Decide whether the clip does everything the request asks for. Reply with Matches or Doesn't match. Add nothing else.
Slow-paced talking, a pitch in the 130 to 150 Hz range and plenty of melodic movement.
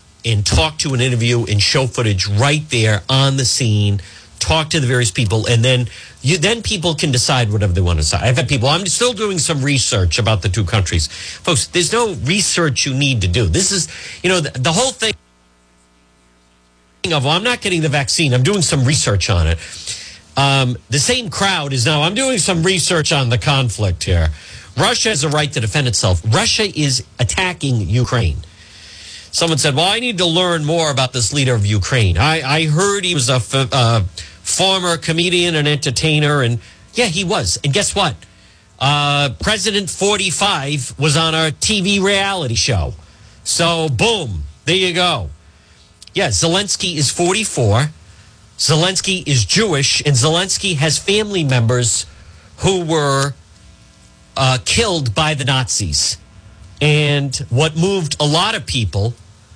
Doesn't match